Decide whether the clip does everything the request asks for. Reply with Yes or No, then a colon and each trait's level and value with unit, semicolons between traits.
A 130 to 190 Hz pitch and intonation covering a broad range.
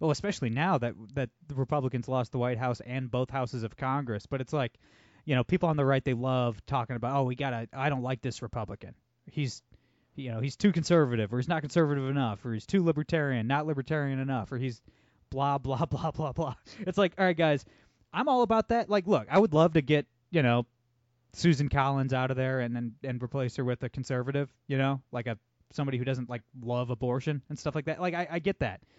No: low, 135 Hz; average, 3.8 semitones